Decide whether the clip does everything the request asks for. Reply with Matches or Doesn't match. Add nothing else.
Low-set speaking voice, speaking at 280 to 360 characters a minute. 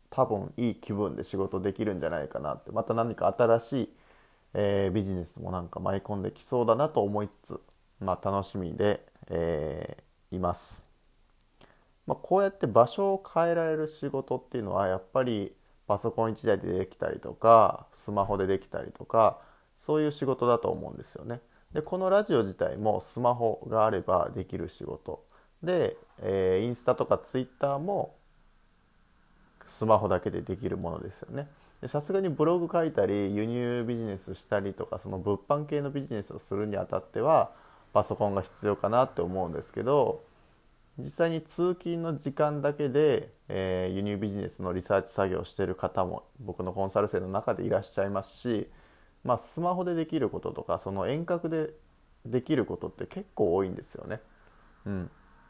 Matches